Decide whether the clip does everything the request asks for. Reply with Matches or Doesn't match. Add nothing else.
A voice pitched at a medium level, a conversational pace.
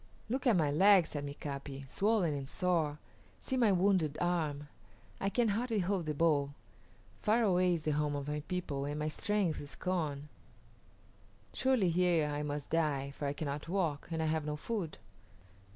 Matches